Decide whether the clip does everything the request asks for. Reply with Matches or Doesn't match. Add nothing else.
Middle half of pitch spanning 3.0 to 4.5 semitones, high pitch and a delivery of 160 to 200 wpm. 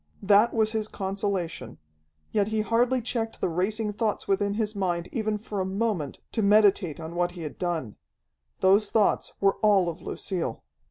Matches